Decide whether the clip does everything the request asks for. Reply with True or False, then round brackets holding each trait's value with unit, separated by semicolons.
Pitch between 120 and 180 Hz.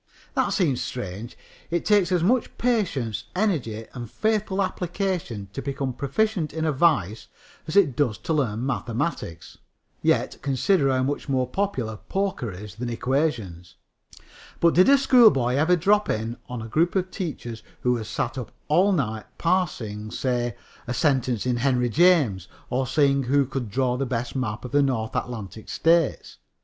True (135 Hz)